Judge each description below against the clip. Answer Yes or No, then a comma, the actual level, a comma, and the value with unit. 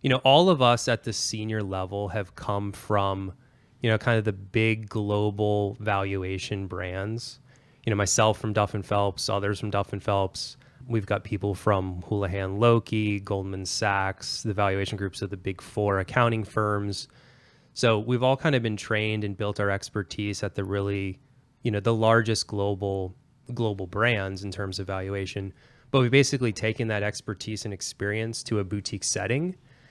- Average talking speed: Yes, average, 175 wpm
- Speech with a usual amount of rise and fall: Yes, average, 3.0 semitones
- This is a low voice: Yes, low, 105 Hz